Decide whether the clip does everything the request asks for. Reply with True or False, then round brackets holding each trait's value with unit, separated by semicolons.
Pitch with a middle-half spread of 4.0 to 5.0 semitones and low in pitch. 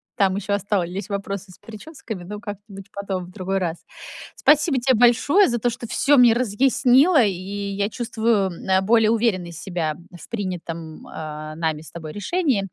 False (4.4 semitones; 200 Hz)